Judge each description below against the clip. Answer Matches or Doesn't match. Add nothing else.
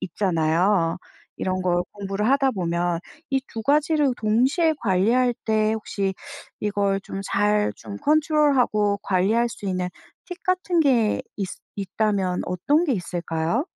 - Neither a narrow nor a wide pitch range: Doesn't match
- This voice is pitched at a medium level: Doesn't match